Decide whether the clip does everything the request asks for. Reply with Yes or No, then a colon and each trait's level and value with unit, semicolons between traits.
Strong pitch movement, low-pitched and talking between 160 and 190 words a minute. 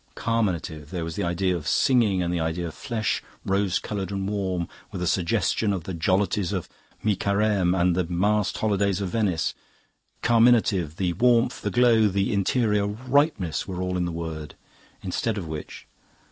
No: average, 3.4 semitones; very low, 95 Hz; average, 175 wpm